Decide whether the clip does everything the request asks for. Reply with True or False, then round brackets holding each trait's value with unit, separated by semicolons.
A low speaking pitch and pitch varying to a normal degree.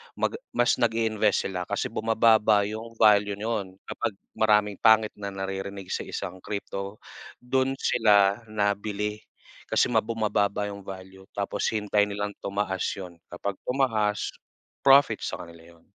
False (105 Hz; 2.0 semitones)